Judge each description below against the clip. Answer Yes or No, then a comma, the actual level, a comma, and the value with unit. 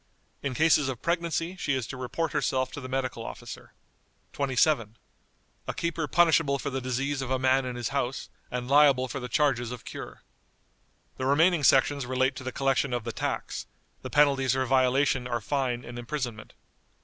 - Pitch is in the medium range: No, low, 130 Hz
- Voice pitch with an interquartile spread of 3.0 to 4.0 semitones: No, narrow, 2.4 semitones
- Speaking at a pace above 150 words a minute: Yes, average, 180 wpm